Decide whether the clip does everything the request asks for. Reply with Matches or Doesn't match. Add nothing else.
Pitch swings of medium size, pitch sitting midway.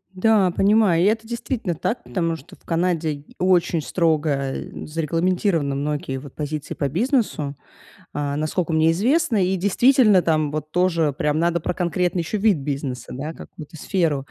Matches